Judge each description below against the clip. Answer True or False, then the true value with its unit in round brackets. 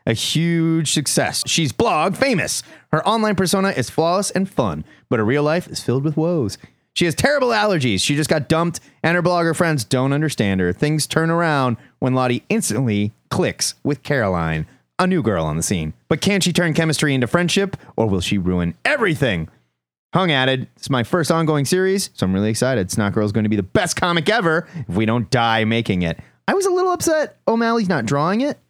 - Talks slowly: False (205 wpm)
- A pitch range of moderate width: False (7.6 semitones)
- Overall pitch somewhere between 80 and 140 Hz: False (150 Hz)